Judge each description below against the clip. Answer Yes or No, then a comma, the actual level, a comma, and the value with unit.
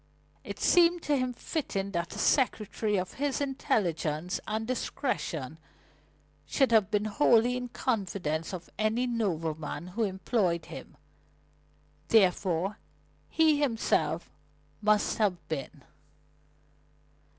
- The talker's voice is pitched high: Yes, high, 210 Hz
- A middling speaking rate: No, slow, 110 wpm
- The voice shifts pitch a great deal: Yes, wide, 6.1 semitones